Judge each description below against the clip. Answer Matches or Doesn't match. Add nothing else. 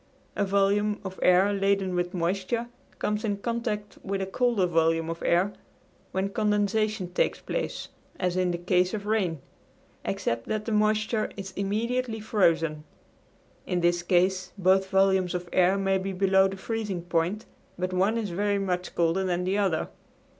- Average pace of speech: Matches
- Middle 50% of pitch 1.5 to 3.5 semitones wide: Matches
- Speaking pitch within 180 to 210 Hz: Matches